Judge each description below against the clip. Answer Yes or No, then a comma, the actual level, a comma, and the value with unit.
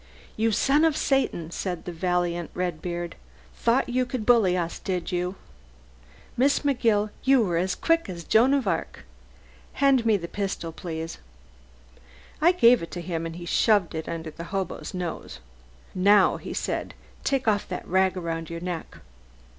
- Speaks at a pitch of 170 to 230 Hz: Yes, medium, 185 Hz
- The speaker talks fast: No, average, 160 wpm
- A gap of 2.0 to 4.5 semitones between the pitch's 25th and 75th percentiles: No, wide, 5.4 semitones